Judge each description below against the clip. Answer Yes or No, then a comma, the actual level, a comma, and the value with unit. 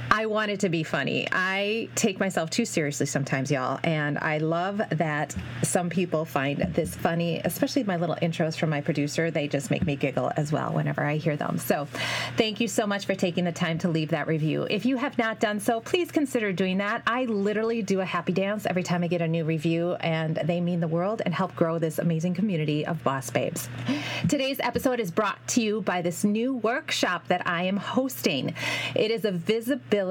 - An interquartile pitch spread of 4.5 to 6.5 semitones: Yes, average, 5.1 semitones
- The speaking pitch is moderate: Yes, medium, 175 Hz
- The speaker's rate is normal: No, fast, 215 wpm